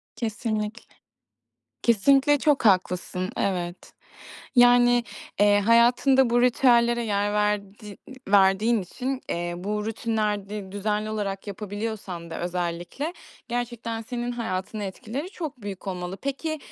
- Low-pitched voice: No, high, 215 Hz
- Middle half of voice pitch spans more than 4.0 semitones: No, average, 3.7 semitones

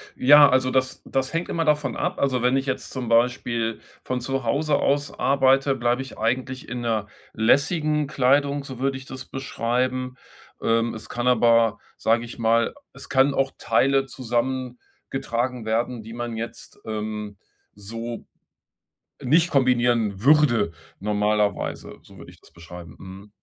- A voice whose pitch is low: Yes, low, 125 Hz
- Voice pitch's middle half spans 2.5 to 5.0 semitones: Yes, average, 2.9 semitones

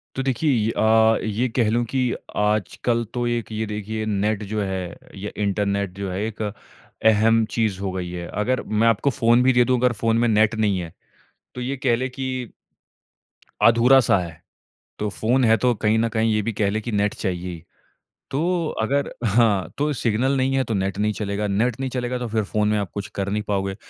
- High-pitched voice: No, low, 110 Hz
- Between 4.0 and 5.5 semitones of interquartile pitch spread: No, average, 3.0 semitones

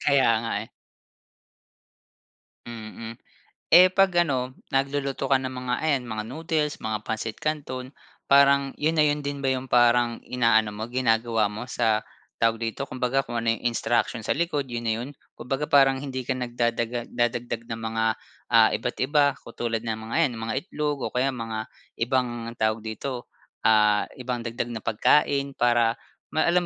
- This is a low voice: Yes, low, 125 Hz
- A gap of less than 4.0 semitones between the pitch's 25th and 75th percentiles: Yes, average, 3.2 semitones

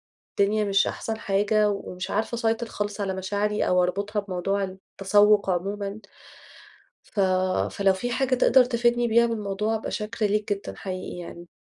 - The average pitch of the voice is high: Yes, high, 205 Hz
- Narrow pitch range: Yes, narrow, 2.2 semitones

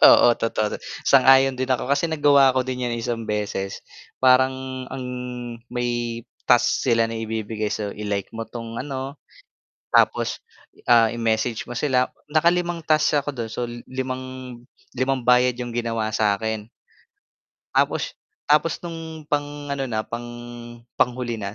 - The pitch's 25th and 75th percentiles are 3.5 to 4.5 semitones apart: No, average, 2.9 semitones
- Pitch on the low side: Yes, low, 125 Hz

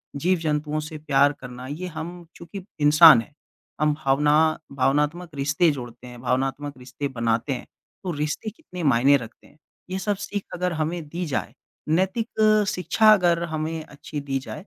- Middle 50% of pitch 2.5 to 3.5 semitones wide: No, average, 4.3 semitones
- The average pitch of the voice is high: No, medium, 150 Hz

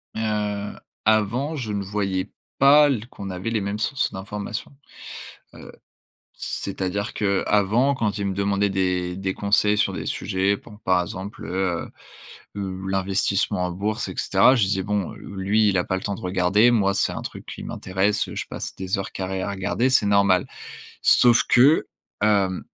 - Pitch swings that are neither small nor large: No, narrow, 1.9 semitones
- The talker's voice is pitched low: Yes, low, 100 Hz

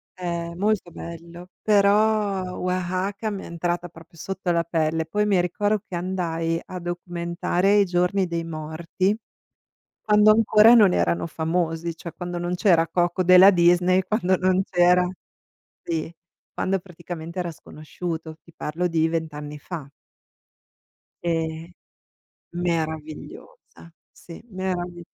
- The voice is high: No, medium, 175 Hz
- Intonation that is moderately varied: No, narrow, 2.0 semitones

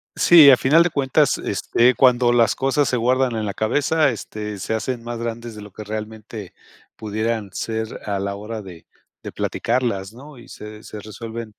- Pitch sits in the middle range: No, low, 115 Hz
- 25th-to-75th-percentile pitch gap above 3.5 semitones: No, average, 2.9 semitones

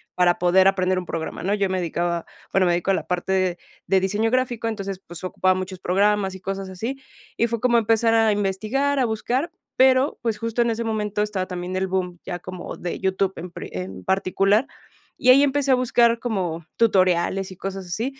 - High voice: Yes, high, 195 Hz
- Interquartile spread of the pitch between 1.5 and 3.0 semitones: No, average, 3.8 semitones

